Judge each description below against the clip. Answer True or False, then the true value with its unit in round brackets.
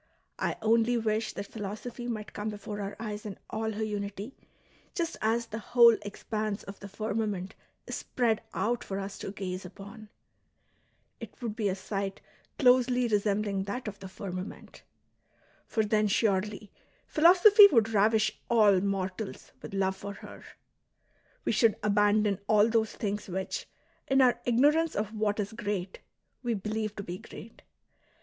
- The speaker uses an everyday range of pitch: False (2.2 semitones)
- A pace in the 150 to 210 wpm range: True (155 wpm)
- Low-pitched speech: False (210 Hz)